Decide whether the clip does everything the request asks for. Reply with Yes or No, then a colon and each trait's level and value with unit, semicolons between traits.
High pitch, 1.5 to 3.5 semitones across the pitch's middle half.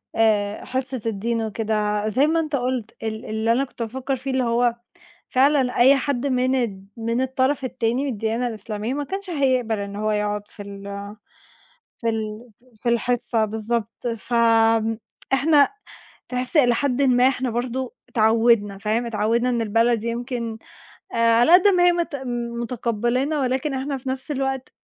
Yes: high, 240 Hz; average, 3.0 semitones